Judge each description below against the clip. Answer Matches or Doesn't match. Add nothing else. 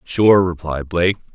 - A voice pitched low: Matches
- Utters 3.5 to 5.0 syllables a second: Matches